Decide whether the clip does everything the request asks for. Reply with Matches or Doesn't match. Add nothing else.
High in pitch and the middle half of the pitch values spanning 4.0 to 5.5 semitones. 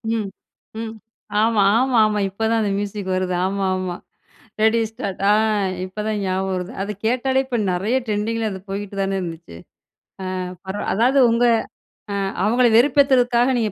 Doesn't match